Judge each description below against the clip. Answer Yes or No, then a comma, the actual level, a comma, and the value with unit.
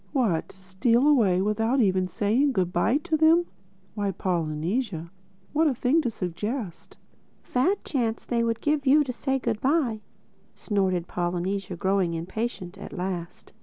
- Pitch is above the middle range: Yes, high, 215 Hz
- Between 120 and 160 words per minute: Yes, average, 150 wpm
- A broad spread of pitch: Yes, wide, 6.2 semitones